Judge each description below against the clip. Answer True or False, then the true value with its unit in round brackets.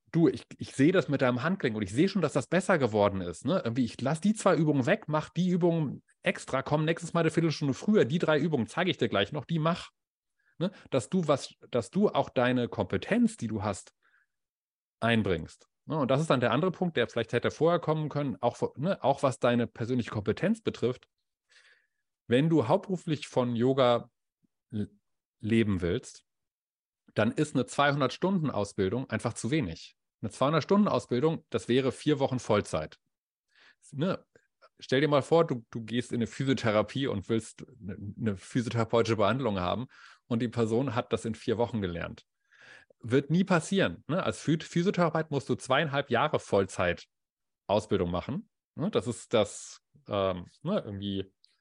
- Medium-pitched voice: False (130 Hz)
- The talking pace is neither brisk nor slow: True (180 wpm)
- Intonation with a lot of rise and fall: True (6.0 semitones)